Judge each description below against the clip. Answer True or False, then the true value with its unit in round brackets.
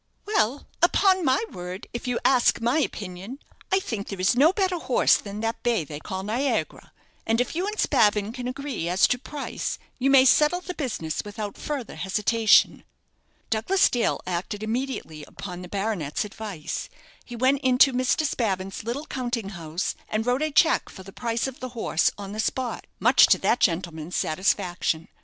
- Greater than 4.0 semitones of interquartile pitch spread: True (5.5 semitones)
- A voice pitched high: True (230 Hz)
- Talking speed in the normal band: True (175 wpm)